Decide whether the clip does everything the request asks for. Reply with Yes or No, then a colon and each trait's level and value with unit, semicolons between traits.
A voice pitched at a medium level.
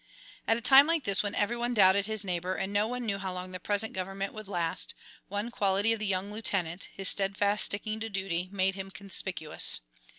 No: high, 200 Hz